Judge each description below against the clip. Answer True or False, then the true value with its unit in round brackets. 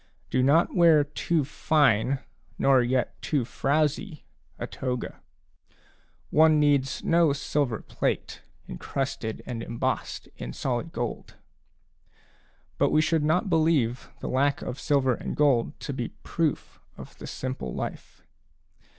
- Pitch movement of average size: True (3.5 semitones)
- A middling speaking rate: False (125 wpm)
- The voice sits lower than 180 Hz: True (140 Hz)